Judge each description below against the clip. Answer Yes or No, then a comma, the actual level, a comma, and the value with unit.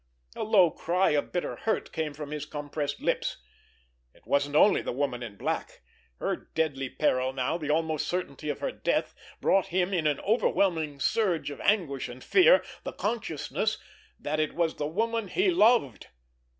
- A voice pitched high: No, medium, 155 Hz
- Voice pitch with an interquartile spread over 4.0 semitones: Yes, average, 5.1 semitones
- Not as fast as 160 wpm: No, average, 170 wpm